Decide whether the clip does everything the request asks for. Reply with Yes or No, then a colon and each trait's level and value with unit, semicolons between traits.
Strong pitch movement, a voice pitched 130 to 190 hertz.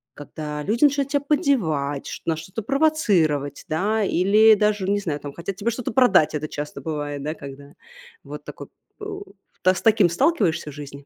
Yes: wide, 7.1 semitones; medium, 185 Hz